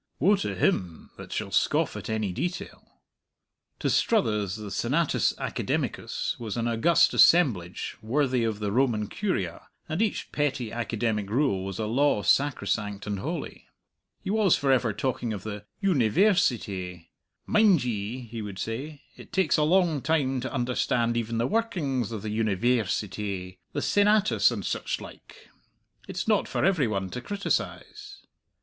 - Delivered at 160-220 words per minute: No, average, 150 wpm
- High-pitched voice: No, low, 120 Hz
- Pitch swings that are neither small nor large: No, wide, 6.9 semitones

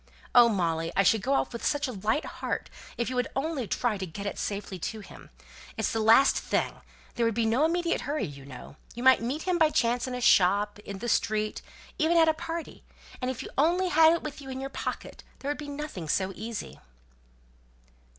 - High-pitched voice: Yes, high, 240 Hz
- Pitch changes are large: Yes, wide, 6.1 semitones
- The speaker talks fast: Yes, fast, 220 wpm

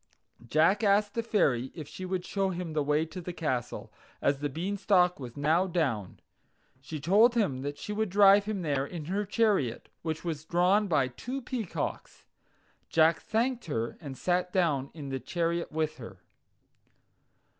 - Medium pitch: Yes, medium, 170 Hz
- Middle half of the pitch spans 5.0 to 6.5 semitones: Yes, wide, 5.5 semitones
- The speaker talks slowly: No, average, 165 wpm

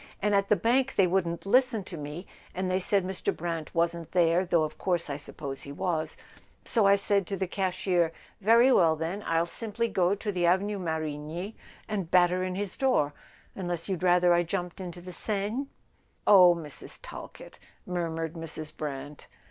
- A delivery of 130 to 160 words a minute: No, average, 185 wpm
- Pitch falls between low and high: Yes, medium, 180 Hz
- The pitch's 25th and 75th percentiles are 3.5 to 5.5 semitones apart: No, average, 3.1 semitones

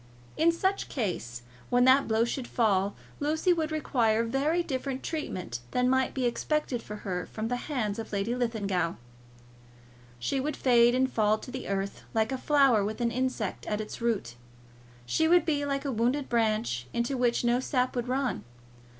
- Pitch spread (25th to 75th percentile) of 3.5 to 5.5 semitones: Yes, average, 4.0 semitones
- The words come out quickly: No, average, 175 wpm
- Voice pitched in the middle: No, high, 245 Hz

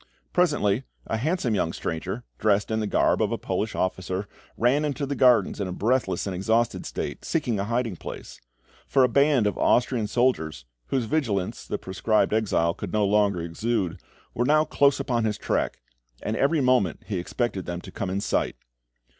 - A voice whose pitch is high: No, low, 110 Hz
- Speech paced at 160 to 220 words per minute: Yes, average, 180 wpm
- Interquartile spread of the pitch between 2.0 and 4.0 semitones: No, average, 4.6 semitones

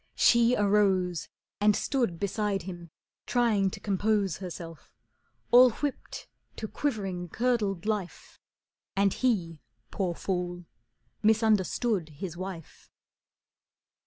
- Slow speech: Yes, slow, 100 wpm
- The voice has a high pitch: Yes, high, 195 Hz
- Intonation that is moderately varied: Yes, average, 3.7 semitones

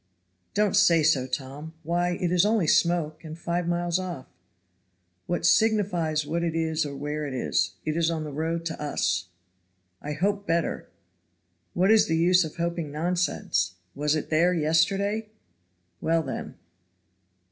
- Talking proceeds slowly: No, average, 155 wpm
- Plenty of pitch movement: No, narrow, 2.6 semitones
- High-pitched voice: No, medium, 165 Hz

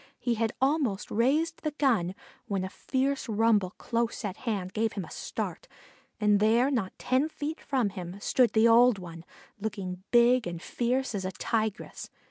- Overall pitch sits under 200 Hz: No, high, 225 Hz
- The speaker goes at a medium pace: Yes, average, 170 wpm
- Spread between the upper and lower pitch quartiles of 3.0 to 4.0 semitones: No, average, 4.6 semitones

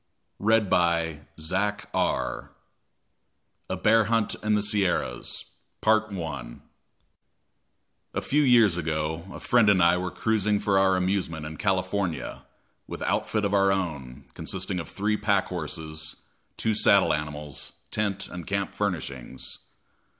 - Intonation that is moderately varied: Yes, average, 4.4 semitones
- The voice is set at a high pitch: No, very low, 95 Hz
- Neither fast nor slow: No, slow, 120 wpm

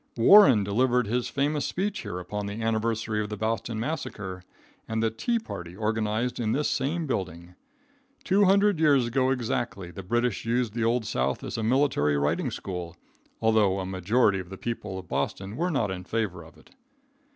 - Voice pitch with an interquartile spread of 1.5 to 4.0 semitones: No, average, 4.8 semitones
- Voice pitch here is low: Yes, low, 110 Hz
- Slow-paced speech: No, average, 180 wpm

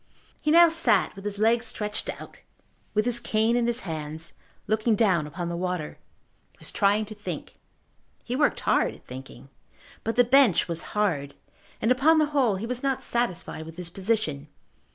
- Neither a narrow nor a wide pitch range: No, wide, 5.9 semitones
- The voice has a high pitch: Yes, high, 215 Hz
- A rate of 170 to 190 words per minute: Yes, average, 180 wpm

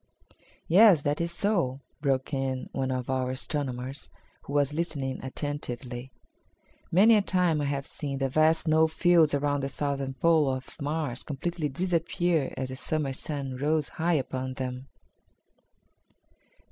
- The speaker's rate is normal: Yes, average, 145 wpm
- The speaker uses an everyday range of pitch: Yes, average, 3.3 semitones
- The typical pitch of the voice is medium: Yes, medium, 145 Hz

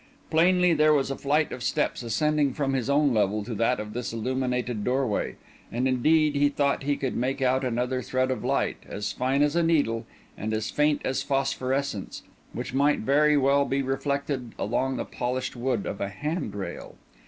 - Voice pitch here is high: No, low, 130 Hz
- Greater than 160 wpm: Yes, average, 185 wpm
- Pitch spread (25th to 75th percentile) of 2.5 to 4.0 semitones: Yes, average, 2.9 semitones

